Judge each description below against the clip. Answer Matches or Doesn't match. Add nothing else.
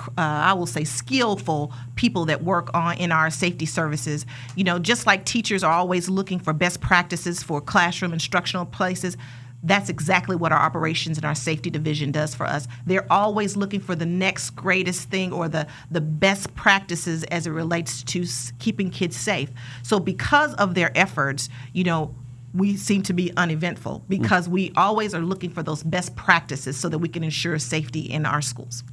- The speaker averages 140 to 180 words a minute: Doesn't match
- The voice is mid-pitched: Matches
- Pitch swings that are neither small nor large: Matches